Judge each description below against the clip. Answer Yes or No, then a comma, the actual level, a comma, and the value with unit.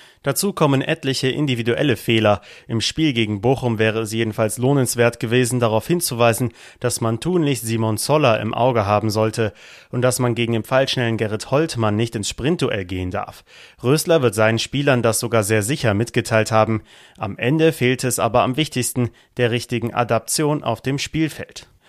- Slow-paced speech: No, average, 165 wpm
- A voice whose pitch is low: Yes, low, 120 Hz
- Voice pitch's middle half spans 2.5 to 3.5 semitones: Yes, average, 2.9 semitones